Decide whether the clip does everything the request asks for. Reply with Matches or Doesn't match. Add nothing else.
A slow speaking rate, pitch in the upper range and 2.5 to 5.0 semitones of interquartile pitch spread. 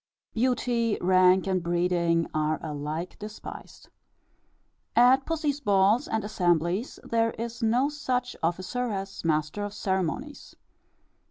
Doesn't match